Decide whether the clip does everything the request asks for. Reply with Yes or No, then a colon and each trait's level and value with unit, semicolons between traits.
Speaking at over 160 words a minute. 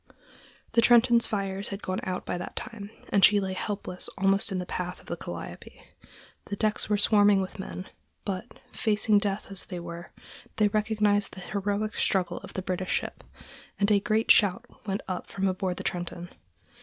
Yes: average, 180 wpm